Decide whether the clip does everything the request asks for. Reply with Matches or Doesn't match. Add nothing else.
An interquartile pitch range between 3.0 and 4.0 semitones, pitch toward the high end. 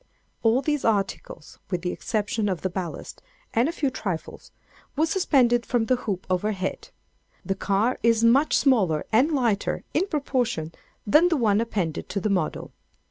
Doesn't match